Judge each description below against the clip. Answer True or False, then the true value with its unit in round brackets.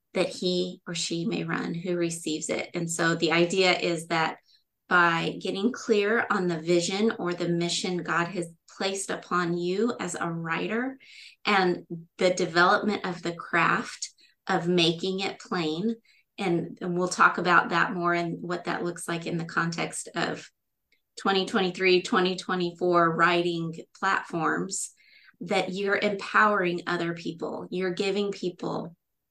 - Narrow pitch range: True (2.2 semitones)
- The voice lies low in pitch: False (180 Hz)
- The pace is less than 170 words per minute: True (145 wpm)